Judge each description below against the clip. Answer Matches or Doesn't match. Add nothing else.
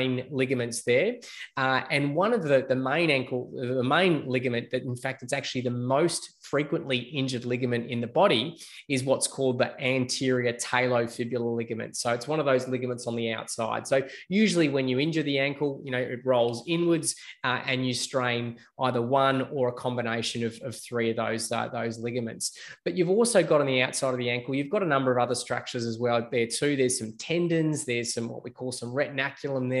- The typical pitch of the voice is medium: Doesn't match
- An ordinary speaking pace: Doesn't match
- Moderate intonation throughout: Doesn't match